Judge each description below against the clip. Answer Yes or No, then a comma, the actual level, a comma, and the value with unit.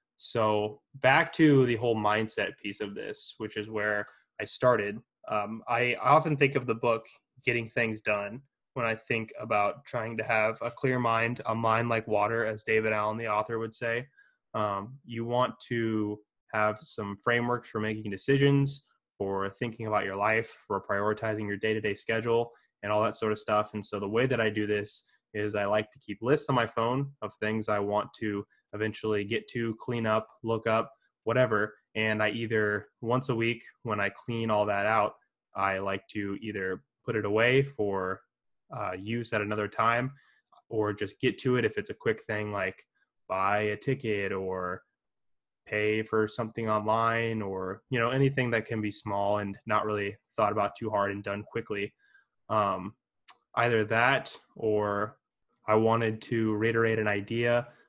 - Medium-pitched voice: No, low, 110 Hz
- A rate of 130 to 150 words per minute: No, average, 180 wpm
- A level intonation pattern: Yes, narrow, 2.0 semitones